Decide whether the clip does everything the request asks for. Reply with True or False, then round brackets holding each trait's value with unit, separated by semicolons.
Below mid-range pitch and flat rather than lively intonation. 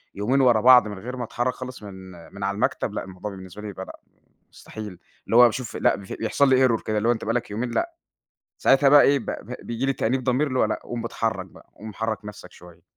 False (115 Hz; 3.6 semitones)